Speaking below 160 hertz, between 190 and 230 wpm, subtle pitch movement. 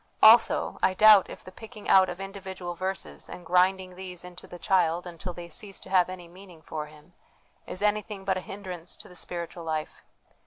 No: medium, 185 Hz; average, 195 wpm; narrow, 1.8 semitones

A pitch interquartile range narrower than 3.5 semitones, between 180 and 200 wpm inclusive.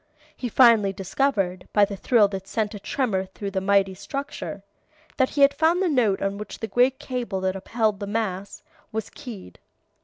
No: average, 4.3 semitones; average, 185 wpm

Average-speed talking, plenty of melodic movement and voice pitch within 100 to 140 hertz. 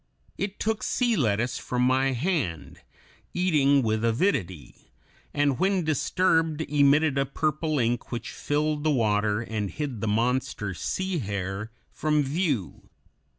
No: slow, 130 wpm; wide, 5.7 semitones; low, 135 Hz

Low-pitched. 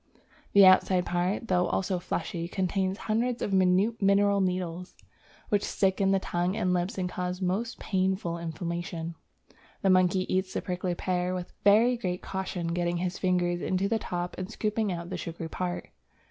No: medium, 185 Hz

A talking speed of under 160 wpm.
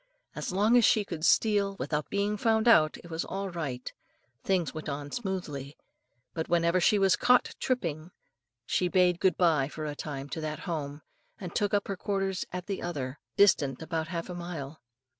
No: average, 185 wpm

